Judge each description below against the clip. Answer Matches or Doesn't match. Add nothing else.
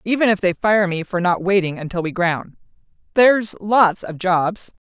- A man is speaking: Doesn't match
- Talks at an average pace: Matches